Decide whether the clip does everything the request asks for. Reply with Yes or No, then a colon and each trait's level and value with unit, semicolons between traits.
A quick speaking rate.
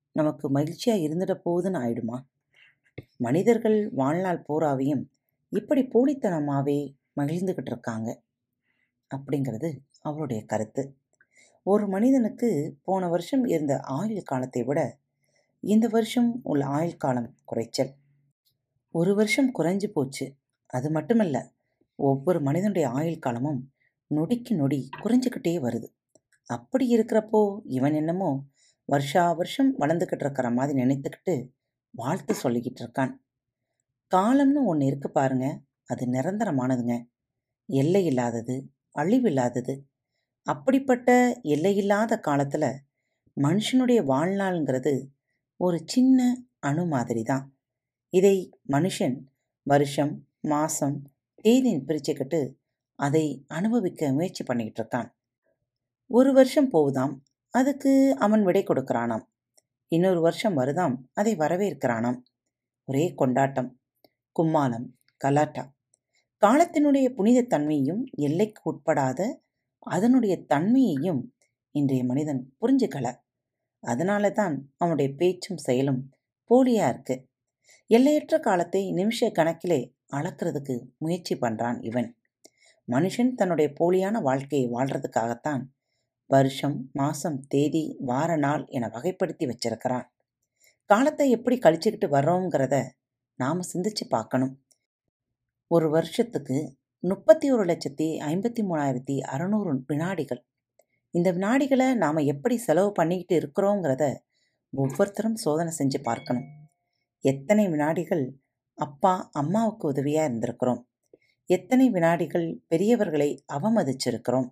No: average, 95 wpm